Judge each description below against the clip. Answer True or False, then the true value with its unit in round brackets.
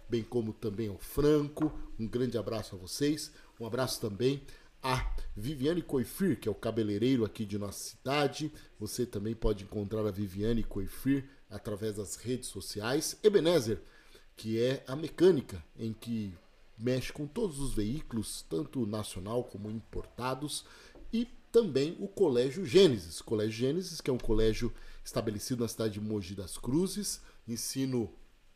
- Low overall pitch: True (120 Hz)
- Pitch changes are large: False (4.7 semitones)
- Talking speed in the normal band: True (150 wpm)